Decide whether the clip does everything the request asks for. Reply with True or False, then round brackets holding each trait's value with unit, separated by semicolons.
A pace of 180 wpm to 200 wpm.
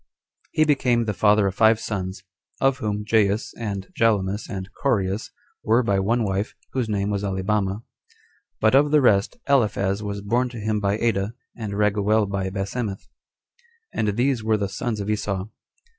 False (170 wpm)